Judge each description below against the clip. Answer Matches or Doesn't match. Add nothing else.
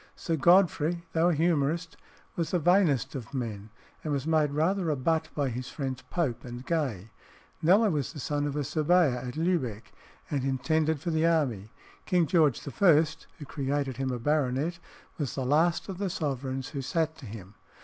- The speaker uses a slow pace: Doesn't match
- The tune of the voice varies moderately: Matches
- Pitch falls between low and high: Matches